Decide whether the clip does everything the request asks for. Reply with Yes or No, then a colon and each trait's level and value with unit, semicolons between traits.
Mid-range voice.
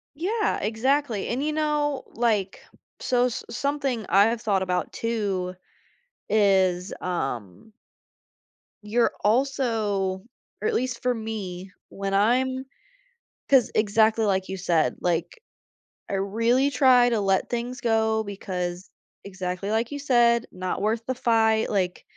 No: high, 220 Hz